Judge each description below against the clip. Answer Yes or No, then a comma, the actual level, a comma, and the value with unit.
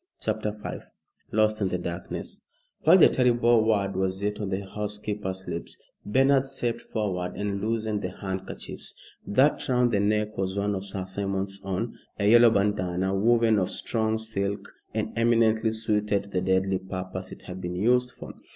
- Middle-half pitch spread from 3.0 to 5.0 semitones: No, narrow, 2.6 semitones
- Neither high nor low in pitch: No, low, 105 Hz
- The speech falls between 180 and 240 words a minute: No, average, 170 wpm